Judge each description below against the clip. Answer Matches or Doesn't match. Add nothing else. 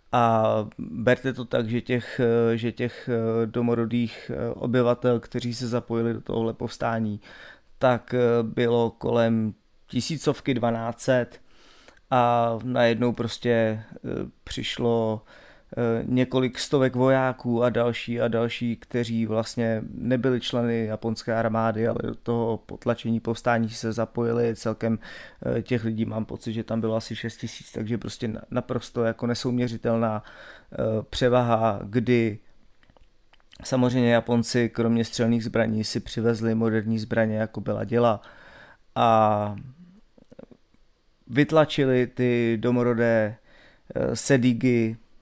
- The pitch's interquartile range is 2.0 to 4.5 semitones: Doesn't match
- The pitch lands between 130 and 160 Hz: Doesn't match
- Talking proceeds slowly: Matches